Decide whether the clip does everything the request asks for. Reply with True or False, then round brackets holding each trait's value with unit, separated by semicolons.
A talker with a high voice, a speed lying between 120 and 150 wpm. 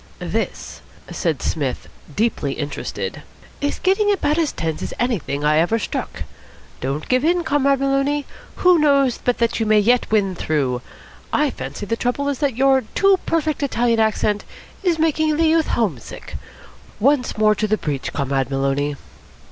False (240 Hz; 165 wpm)